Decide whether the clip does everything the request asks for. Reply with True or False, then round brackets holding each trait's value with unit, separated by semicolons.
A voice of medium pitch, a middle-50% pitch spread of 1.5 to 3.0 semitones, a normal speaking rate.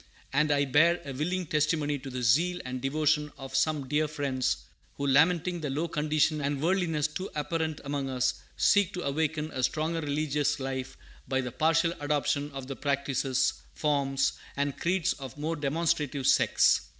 True (145 Hz; 2.6 semitones; 165 wpm)